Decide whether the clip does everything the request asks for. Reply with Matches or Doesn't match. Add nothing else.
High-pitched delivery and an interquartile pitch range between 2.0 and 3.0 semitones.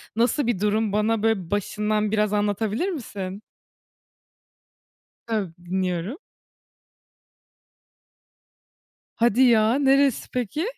Matches